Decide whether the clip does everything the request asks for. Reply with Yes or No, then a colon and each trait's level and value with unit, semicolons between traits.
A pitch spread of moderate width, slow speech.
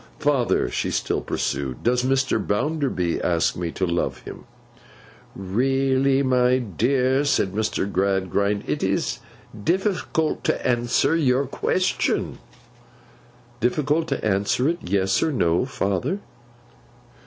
No: wide, 5.9 semitones; slow, 115 wpm